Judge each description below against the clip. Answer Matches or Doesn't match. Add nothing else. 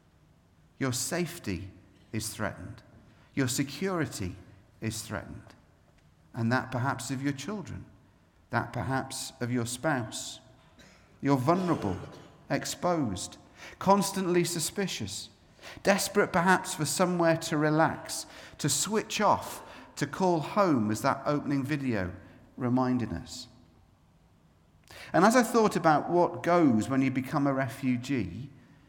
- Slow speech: Matches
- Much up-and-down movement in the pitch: Matches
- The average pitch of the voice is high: Doesn't match